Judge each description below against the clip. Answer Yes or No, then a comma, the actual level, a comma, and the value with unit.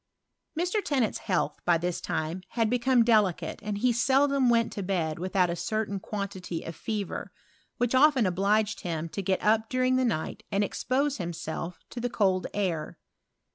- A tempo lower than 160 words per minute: No, average, 175 wpm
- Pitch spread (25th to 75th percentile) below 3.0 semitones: No, average, 5.2 semitones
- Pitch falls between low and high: No, high, 210 Hz